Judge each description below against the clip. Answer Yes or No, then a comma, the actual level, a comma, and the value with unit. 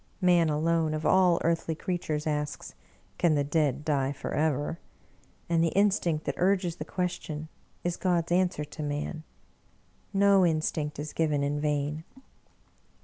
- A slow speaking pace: No, average, 145 wpm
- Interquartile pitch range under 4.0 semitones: Yes, average, 2.9 semitones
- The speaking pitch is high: No, medium, 160 Hz